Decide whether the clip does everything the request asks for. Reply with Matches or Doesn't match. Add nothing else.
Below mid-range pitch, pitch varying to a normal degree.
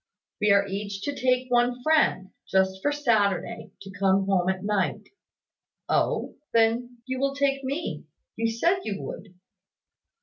Doesn't match